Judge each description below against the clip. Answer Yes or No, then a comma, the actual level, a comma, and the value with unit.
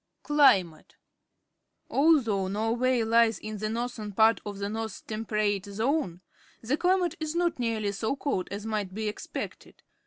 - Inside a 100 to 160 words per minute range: Yes, average, 150 wpm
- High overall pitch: Yes, high, 220 Hz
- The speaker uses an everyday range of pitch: Yes, average, 3.8 semitones